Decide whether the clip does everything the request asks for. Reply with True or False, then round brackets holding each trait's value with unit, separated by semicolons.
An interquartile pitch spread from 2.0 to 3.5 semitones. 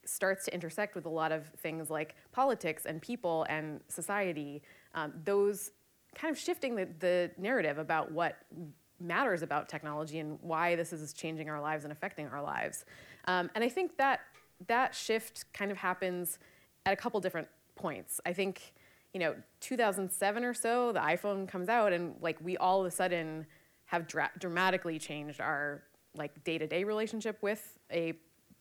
False (4.3 semitones)